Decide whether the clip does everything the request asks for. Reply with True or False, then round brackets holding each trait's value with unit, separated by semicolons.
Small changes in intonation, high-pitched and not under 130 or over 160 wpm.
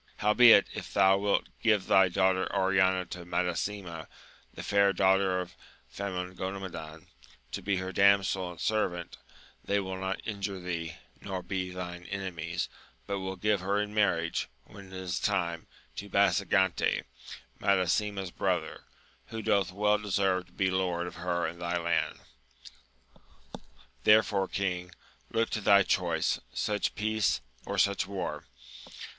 False (2.0 semitones; 95 Hz; 140 wpm)